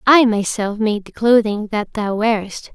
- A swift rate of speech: No, average, 175 wpm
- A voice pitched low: No, high, 215 Hz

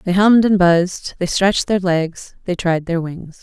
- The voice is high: No, medium, 180 Hz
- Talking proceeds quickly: Yes, fast, 210 wpm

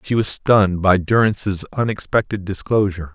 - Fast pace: No, slow, 135 wpm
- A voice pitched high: No, low, 100 Hz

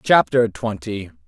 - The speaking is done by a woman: No, male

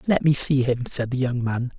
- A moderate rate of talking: No, fast, 270 wpm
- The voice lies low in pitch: Yes, low, 130 Hz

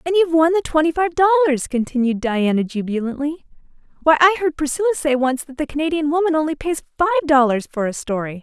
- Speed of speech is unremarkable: Yes, average, 190 wpm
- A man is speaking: No, female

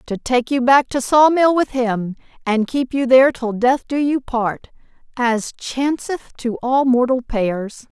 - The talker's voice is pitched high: Yes, very high, 255 Hz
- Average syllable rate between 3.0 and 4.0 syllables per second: Yes, 3.9 syllables/s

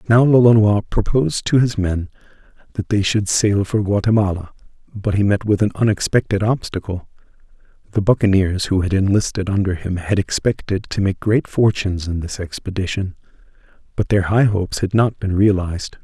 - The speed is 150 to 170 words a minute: Yes, average, 160 wpm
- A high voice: No, low, 100 Hz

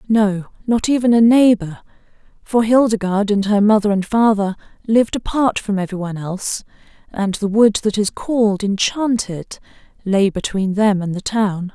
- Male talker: No, female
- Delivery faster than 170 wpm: No, average, 160 wpm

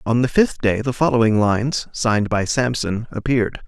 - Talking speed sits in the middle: Yes, average, 180 wpm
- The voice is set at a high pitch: No, low, 120 Hz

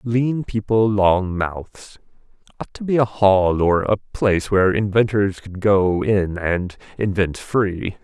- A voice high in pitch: No, low, 100 Hz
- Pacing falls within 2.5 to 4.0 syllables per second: Yes, 3.7 syllables/s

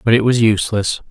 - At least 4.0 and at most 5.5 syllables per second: No, 6.3 syllables/s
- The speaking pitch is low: Yes, low, 110 Hz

